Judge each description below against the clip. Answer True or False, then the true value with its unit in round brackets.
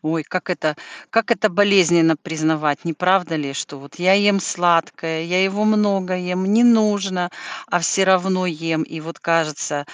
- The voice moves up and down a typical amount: True (3.2 semitones)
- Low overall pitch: False (175 Hz)